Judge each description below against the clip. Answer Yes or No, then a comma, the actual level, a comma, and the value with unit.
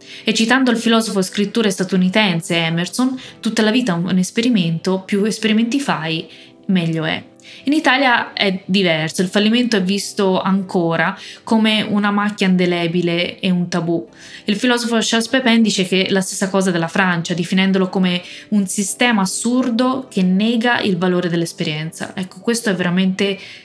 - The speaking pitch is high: Yes, high, 195 Hz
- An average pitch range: Yes, average, 3.8 semitones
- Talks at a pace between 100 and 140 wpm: No, average, 150 wpm